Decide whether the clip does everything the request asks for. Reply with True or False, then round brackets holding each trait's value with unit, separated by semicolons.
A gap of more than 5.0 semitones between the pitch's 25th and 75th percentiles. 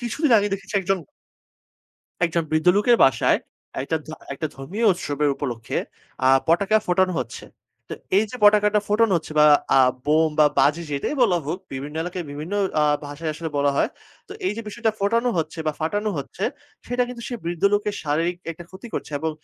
True (5.5 semitones)